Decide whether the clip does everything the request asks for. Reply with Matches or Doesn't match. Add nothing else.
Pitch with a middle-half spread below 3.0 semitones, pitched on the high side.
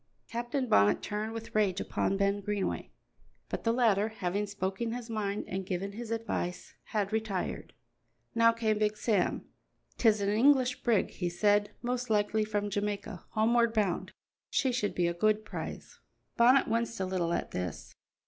Matches